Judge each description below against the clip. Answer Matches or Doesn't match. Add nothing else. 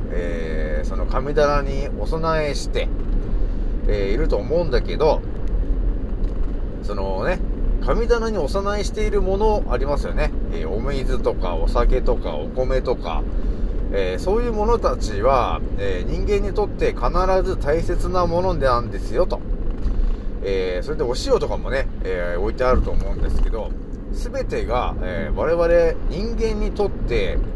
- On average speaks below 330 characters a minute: Matches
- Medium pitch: Matches